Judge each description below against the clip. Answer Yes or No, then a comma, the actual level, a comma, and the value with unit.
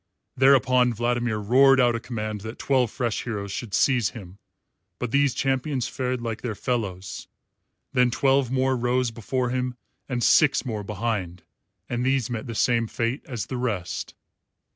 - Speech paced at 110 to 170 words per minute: Yes, average, 160 wpm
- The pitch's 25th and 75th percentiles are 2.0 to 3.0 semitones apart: Yes, average, 2.7 semitones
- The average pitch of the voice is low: Yes, low, 120 Hz